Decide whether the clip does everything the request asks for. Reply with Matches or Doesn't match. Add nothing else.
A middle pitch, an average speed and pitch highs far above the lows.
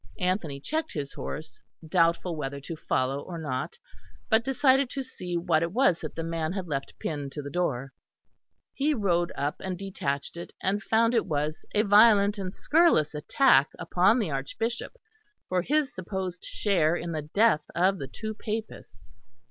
Matches